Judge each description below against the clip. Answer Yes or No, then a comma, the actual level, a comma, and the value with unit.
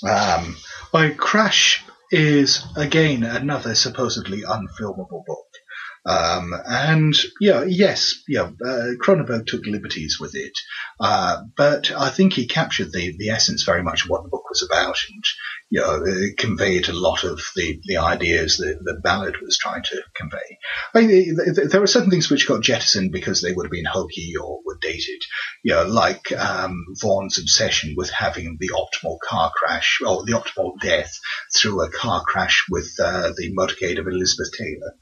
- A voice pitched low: No, medium, 145 Hz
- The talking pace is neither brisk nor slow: Yes, average, 180 wpm